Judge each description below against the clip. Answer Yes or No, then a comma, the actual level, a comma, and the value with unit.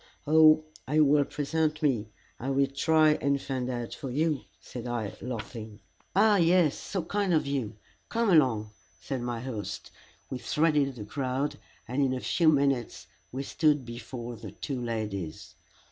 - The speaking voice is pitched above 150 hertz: No, low, 135 Hz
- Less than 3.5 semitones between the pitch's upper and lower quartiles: No, average, 4.3 semitones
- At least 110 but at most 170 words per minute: Yes, average, 160 wpm